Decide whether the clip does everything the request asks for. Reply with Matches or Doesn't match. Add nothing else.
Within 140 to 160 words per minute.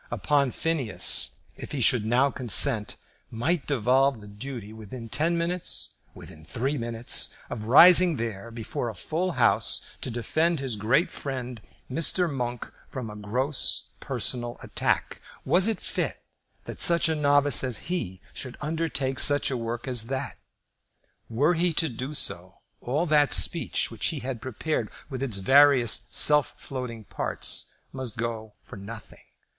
Matches